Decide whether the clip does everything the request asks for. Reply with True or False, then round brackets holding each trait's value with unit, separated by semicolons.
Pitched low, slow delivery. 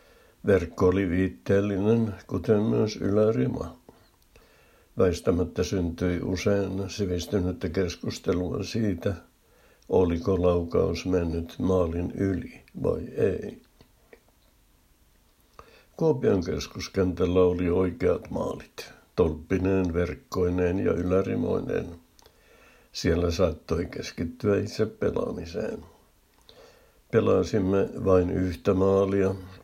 True (95 Hz; 75 wpm)